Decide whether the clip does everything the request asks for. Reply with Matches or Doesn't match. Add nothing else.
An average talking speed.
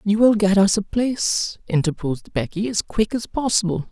Matches